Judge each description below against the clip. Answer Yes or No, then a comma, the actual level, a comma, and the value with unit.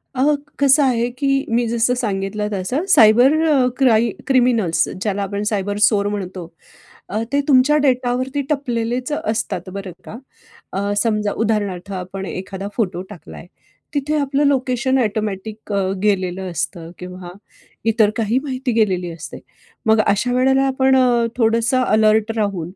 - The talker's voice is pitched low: No, high, 225 Hz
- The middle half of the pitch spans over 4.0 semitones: Yes, average, 4.4 semitones